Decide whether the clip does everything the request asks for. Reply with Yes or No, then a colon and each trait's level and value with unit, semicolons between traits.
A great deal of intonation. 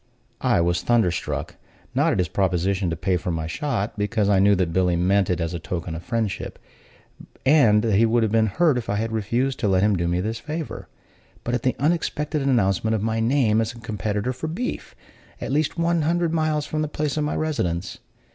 Yes: wide, 6.9 semitones